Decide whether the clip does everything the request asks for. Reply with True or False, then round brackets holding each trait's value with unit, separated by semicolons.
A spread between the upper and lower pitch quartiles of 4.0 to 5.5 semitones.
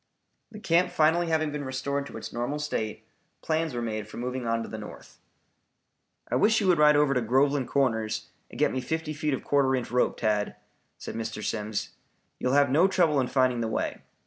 True (4.7 semitones)